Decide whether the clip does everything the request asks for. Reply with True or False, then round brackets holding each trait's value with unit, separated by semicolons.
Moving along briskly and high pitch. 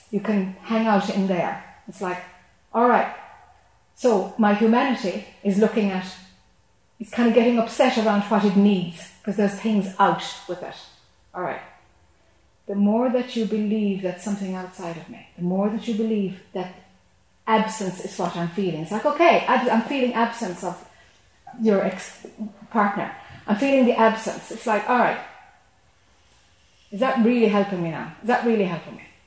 False (170 wpm; 205 Hz)